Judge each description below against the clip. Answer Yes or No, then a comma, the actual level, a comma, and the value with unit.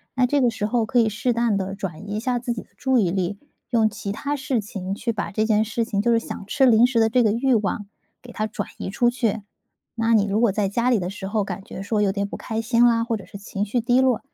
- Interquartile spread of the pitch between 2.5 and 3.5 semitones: Yes, average, 2.9 semitones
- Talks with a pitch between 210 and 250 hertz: Yes, high, 220 Hz